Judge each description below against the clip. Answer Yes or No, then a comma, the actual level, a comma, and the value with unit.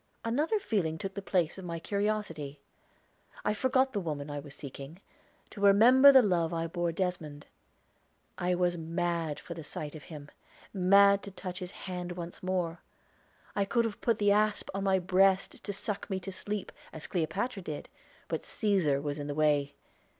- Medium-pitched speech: Yes, medium, 180 Hz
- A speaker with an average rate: Yes, average, 180 wpm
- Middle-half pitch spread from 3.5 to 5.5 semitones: Yes, average, 4.0 semitones